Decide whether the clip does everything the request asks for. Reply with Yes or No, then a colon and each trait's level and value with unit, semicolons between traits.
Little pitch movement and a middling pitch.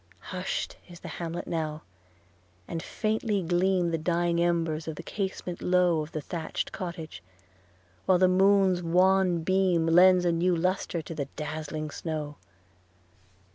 Yes: narrow, 2.2 semitones; medium, 175 Hz